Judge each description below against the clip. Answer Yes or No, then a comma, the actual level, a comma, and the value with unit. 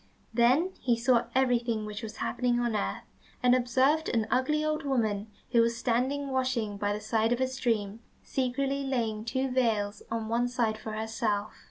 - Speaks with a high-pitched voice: Yes, high, 240 Hz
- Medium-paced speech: Yes, average, 175 wpm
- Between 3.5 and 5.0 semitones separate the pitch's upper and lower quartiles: No, average, 2.9 semitones